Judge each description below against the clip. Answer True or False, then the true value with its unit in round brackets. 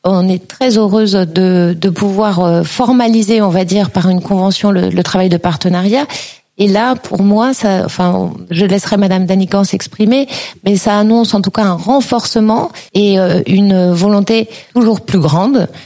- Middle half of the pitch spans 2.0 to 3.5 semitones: True (2.8 semitones)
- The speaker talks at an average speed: True (165 wpm)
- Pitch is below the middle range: False (200 Hz)